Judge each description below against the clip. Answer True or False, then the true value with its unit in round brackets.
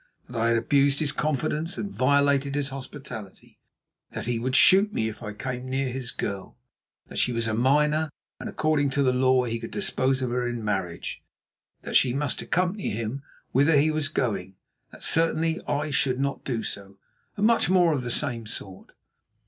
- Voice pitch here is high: False (130 Hz)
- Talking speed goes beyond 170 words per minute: True (190 wpm)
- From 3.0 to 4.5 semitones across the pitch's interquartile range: True (4.2 semitones)